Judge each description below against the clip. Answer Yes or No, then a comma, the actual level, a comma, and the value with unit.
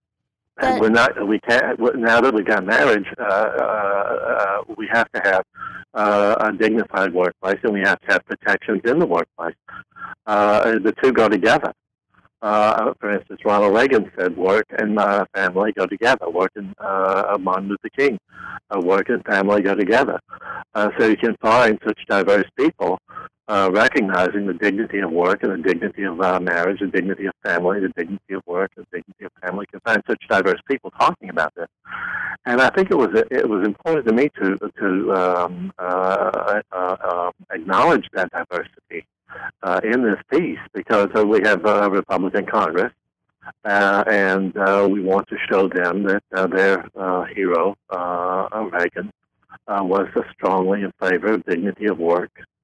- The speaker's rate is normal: Yes, average, 175 wpm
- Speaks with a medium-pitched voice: No, very low, 95 Hz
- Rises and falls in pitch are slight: Yes, narrow, 1.8 semitones